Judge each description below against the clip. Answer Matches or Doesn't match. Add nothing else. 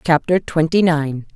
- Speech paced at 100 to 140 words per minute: Matches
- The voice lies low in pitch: Doesn't match